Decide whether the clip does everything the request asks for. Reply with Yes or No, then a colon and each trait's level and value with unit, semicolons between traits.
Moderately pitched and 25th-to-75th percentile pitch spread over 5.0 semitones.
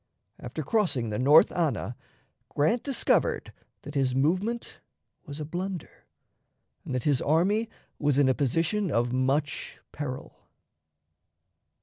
Yes: medium, 150 Hz; wide, 5.4 semitones